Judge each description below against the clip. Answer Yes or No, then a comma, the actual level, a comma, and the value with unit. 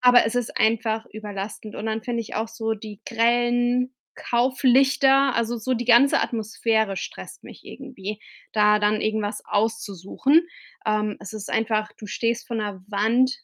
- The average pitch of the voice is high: Yes, high, 225 Hz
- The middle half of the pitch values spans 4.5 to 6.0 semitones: No, narrow, 2.4 semitones